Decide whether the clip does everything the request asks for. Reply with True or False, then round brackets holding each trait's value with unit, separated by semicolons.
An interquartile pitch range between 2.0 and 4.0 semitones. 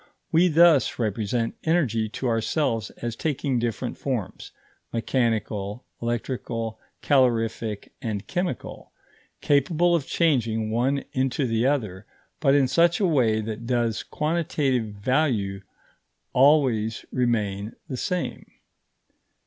False (4.4 semitones)